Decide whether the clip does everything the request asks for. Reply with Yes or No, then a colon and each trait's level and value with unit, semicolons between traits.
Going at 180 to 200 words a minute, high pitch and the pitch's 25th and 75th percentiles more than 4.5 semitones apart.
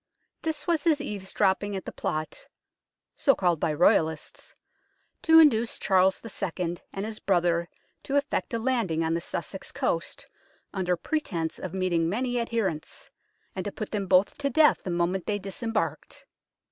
No: average, 155 wpm; high, 195 Hz; average, 5.2 semitones